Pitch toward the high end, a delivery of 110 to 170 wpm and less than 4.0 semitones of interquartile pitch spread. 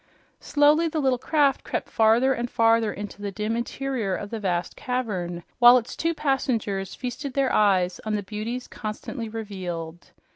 No: high, 225 Hz; average, 160 wpm; average, 4.3 semitones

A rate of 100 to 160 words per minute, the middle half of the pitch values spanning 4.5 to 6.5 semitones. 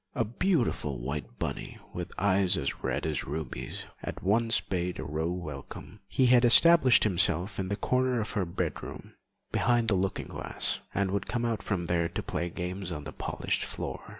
No: average, 175 wpm; average, 5.3 semitones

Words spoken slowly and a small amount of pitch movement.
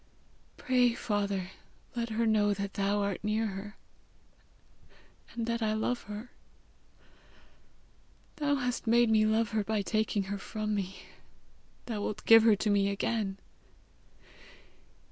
Yes: slow, 130 wpm; narrow, 2.2 semitones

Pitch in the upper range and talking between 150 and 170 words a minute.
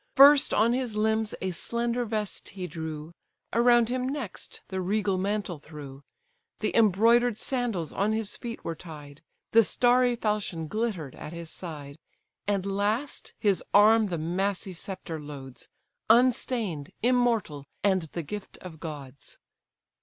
No: high, 205 Hz; average, 140 wpm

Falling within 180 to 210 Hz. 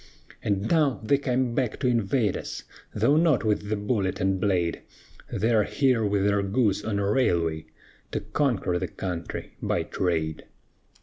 No: low, 105 Hz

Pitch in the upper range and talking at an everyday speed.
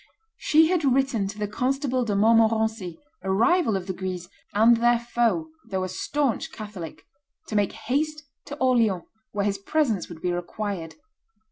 Yes: high, 220 Hz; average, 160 wpm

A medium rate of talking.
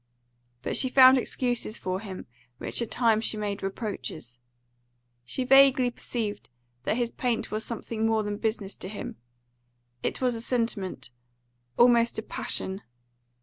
Yes: average, 145 wpm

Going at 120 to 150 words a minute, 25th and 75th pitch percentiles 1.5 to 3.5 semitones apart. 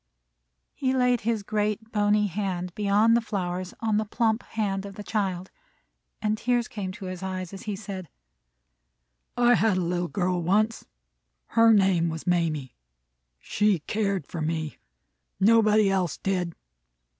Yes: average, 145 wpm; average, 3.1 semitones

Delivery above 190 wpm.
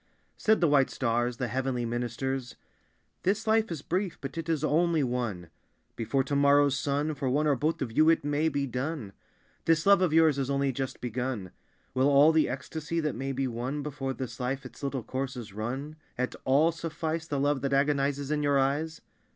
Yes: average, 200 wpm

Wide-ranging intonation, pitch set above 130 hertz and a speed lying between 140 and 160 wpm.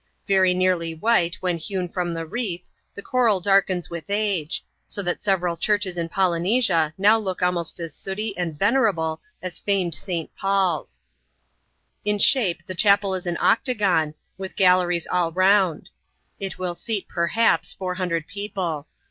No: average, 2.8 semitones; medium, 185 Hz; average, 150 wpm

